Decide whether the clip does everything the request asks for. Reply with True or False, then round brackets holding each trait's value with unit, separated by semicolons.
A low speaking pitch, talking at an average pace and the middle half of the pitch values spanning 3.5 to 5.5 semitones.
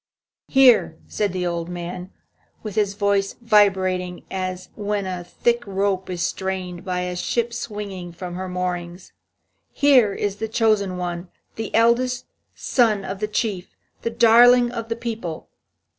False (195 Hz; 145 wpm; 3.8 semitones)